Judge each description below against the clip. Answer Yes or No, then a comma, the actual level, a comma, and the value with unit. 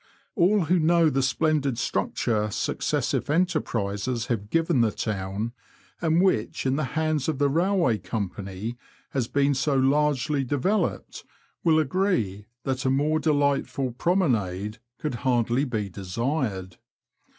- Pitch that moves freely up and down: Yes, wide, 5.9 semitones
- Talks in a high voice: No, low, 135 Hz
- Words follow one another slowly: Yes, slow, 130 wpm